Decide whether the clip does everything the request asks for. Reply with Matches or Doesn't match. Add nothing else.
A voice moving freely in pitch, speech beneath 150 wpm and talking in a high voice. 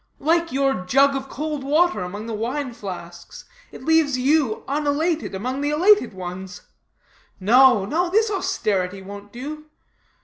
Matches